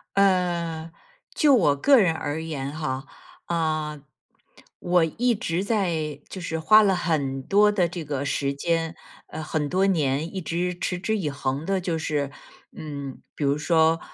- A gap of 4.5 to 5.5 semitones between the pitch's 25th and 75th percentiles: No, average, 3.5 semitones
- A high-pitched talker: No, medium, 165 Hz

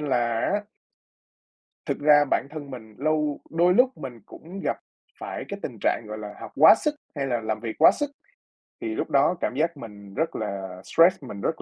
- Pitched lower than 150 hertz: Yes, medium, 140 Hz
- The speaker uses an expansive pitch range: Yes, wide, 6.6 semitones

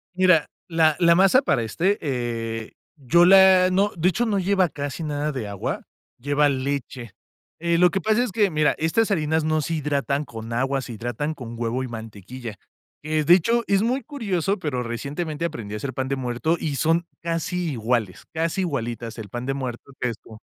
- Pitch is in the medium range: Yes, medium, 150 Hz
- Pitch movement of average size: No, wide, 6.2 semitones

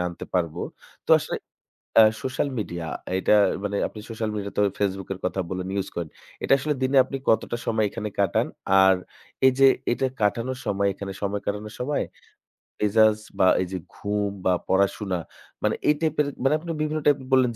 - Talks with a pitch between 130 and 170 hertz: No, low, 105 Hz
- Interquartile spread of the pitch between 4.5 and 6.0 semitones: Yes, average, 4.9 semitones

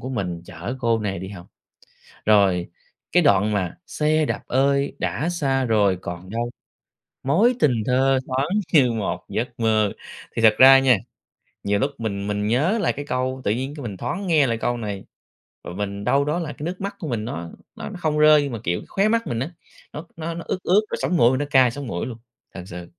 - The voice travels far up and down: Yes, wide, 6.1 semitones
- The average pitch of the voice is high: No, low, 125 Hz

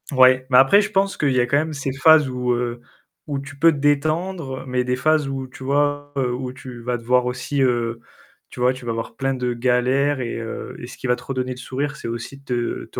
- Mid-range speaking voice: No, low, 130 Hz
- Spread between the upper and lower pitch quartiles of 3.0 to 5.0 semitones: No, narrow, 2.5 semitones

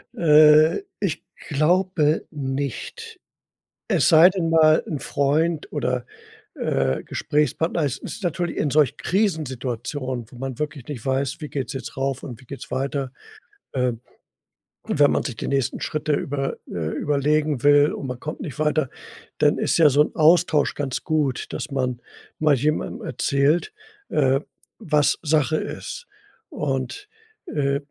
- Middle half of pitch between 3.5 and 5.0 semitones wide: No, average, 2.7 semitones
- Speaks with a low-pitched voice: No, medium, 145 Hz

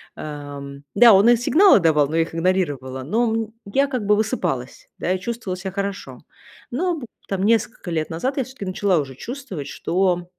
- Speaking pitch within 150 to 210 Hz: Yes, high, 190 Hz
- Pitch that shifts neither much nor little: No, wide, 6.3 semitones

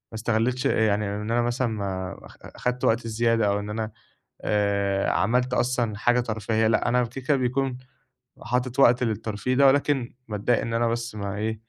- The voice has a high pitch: No, low, 115 Hz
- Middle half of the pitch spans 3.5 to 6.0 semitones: No, average, 2.8 semitones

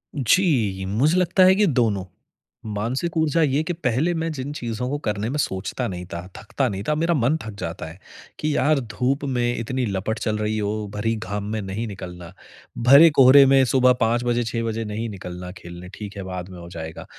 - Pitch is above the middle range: No, low, 115 Hz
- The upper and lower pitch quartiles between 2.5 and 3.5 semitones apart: No, average, 5.3 semitones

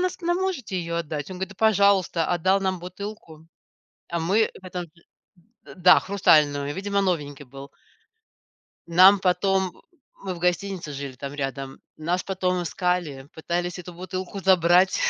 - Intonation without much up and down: No, average, 3.2 semitones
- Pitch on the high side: No, medium, 180 Hz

